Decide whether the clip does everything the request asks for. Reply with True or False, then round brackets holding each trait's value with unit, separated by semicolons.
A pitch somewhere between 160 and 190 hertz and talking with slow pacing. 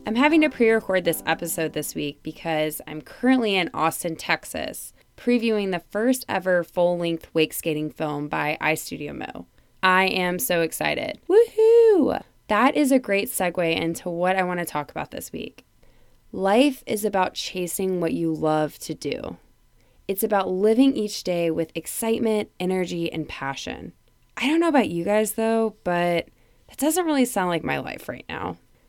False (185 Hz; 165 wpm)